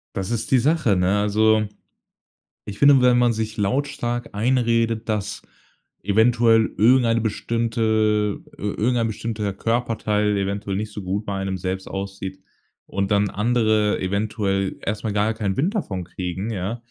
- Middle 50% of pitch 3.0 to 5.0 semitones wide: No, narrow, 2.6 semitones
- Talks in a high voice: No, low, 110 Hz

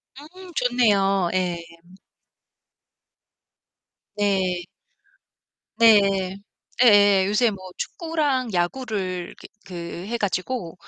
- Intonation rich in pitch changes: No, average, 4.8 semitones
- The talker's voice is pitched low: No, high, 205 Hz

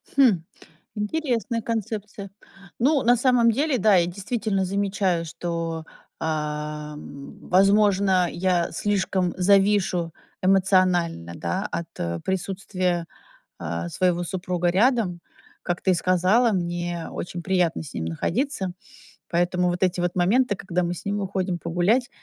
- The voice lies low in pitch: No, medium, 185 Hz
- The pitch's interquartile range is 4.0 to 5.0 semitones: No, average, 3.0 semitones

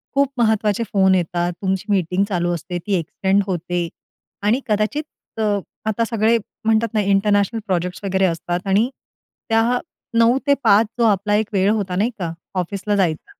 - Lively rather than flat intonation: No, average, 3.4 semitones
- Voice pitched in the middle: No, high, 200 Hz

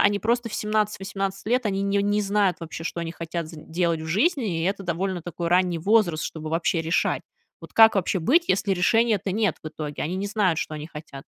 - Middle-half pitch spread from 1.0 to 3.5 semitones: No, average, 4.0 semitones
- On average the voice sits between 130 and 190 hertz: Yes, medium, 185 Hz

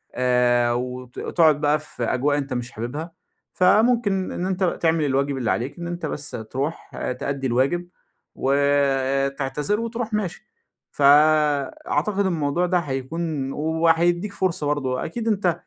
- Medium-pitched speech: Yes, medium, 150 Hz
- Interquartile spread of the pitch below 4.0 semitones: No, average, 4.5 semitones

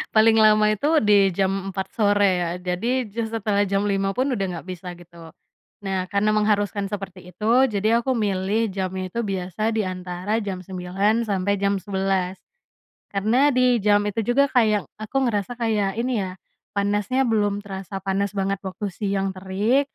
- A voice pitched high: Yes, high, 200 Hz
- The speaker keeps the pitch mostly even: Yes, narrow, 2.3 semitones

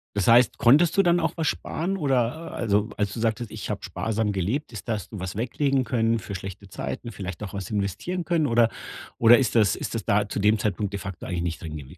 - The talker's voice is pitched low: Yes, low, 110 Hz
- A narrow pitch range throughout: No, average, 4.0 semitones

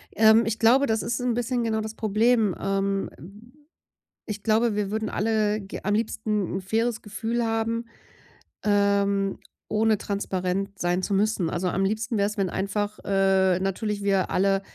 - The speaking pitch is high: Yes, high, 210 Hz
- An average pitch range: No, narrow, 2.2 semitones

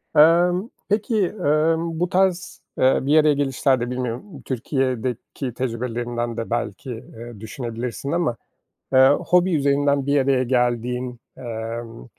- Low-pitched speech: Yes, low, 130 Hz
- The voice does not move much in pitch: No, average, 4.3 semitones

